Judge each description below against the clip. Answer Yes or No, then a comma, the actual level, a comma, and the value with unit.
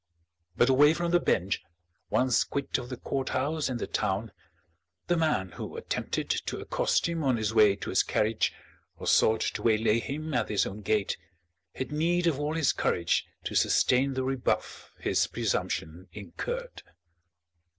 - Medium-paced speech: Yes, average, 160 wpm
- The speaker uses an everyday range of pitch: No, wide, 5.7 semitones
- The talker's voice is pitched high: No, low, 125 Hz